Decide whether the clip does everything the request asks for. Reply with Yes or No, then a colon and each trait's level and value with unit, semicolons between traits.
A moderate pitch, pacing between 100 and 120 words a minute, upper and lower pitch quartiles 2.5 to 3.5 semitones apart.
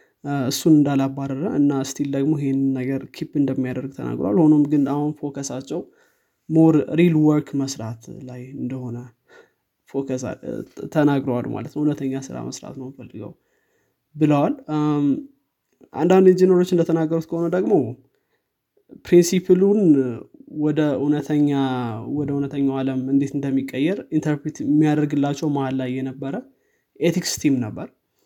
Yes: medium, 145 Hz; average, 105 wpm; average, 2.8 semitones